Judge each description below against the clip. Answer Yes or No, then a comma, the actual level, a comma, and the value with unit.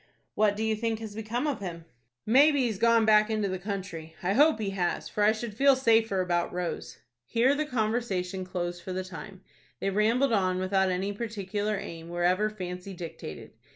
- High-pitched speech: Yes, high, 205 Hz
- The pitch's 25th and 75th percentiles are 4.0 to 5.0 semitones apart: No, average, 3.5 semitones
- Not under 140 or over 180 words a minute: No, average, 190 wpm